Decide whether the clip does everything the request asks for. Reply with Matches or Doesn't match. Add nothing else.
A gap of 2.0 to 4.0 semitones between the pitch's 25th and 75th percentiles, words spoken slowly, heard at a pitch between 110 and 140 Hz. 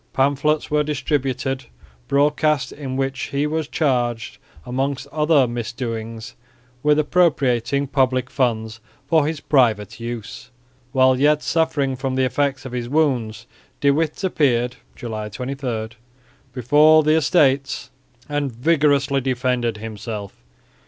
Matches